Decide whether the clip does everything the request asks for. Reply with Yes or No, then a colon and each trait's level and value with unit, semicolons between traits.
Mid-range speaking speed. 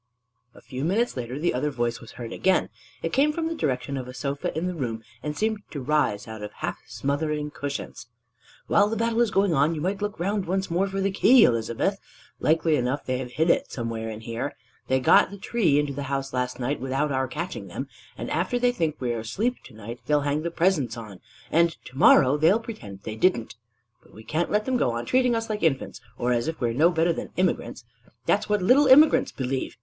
No: fast, 230 wpm